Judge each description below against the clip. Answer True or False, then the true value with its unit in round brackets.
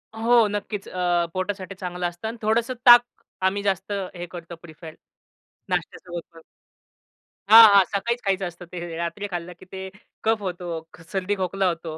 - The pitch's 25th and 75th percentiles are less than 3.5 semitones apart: True (2.9 semitones)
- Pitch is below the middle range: False (185 Hz)